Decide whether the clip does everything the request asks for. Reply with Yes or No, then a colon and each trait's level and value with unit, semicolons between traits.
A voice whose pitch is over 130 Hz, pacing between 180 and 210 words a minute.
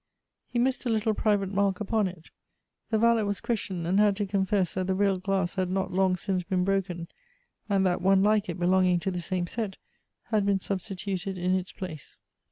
Yes: high, 190 Hz; fast, 205 wpm